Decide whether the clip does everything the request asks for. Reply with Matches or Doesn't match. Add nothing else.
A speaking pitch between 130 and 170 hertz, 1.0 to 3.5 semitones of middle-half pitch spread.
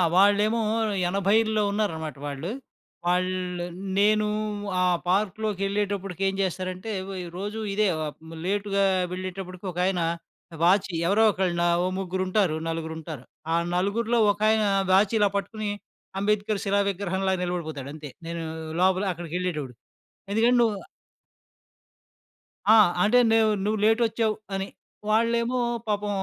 Doesn't match